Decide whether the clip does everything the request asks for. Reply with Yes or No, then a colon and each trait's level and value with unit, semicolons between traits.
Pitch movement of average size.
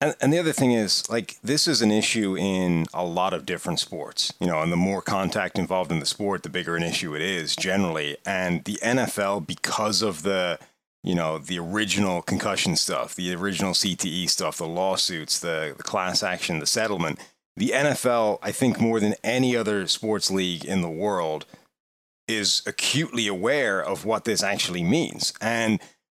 Yes: average, 3.8 semitones